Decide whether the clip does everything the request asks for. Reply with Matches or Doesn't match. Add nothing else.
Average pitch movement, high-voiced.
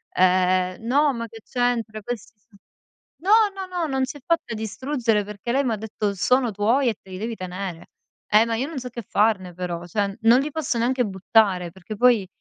Matches